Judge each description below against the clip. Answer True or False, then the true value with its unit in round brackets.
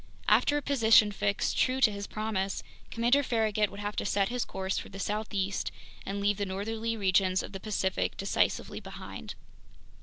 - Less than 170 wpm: False (175 wpm)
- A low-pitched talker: False (205 Hz)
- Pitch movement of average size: False (2.3 semitones)